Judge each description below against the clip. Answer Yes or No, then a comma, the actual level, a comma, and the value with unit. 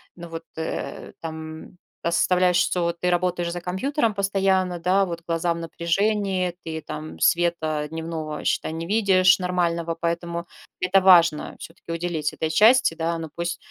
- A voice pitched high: No, medium, 170 Hz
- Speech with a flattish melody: Yes, narrow, 2.0 semitones